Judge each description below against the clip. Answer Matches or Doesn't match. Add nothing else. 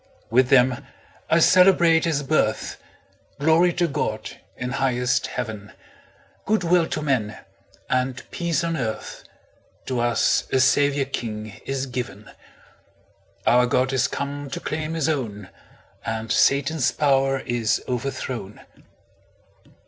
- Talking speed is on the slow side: Matches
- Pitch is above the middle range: Doesn't match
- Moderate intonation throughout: Matches